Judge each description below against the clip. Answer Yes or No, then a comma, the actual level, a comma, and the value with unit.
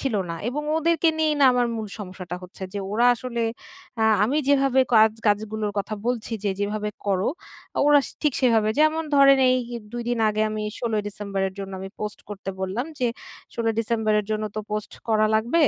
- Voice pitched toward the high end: Yes, high, 220 Hz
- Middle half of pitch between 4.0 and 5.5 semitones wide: No, average, 3.5 semitones